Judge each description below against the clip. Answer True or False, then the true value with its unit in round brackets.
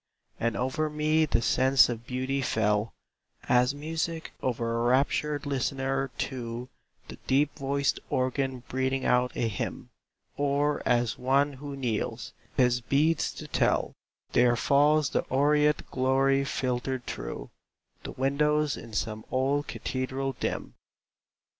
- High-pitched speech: False (135 Hz)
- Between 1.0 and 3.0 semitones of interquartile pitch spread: True (2.5 semitones)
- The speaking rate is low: True (130 wpm)